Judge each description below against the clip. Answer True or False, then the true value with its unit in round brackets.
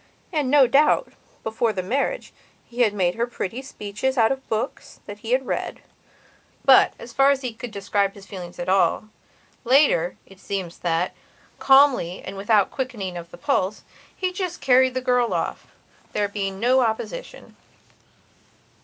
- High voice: True (225 Hz)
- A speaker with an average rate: True (160 wpm)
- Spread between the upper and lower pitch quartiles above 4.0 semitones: True (5.2 semitones)